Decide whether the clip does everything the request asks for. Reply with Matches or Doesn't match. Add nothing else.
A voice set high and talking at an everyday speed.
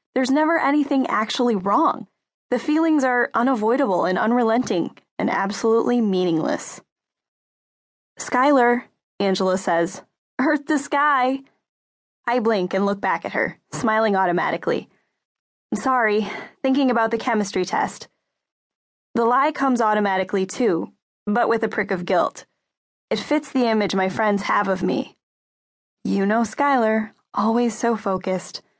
Doesn't match